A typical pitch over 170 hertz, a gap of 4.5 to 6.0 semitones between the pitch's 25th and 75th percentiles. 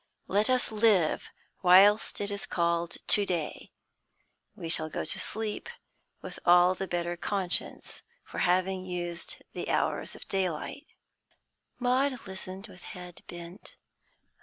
No: medium, 185 Hz; average, 3.0 semitones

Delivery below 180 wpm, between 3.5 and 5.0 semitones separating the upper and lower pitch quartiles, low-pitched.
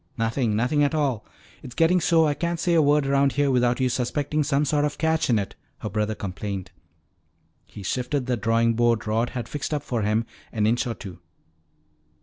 No: fast, 205 wpm; average, 4.5 semitones; low, 125 Hz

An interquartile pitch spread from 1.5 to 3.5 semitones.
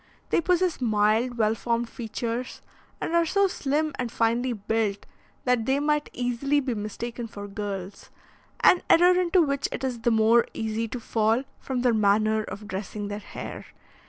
No: average, 4.0 semitones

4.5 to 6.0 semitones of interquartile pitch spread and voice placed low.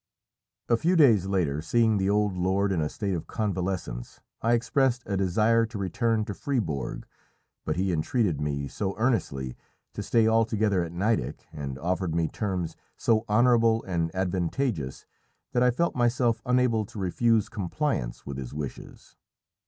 Yes: wide, 5.4 semitones; low, 100 Hz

